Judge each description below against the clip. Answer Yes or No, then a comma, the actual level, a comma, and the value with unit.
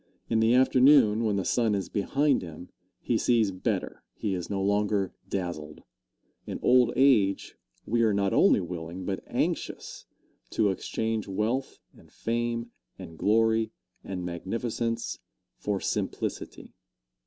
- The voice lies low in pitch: Yes, low, 105 Hz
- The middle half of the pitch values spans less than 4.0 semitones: Yes, average, 3.5 semitones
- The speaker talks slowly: Yes, slow, 130 wpm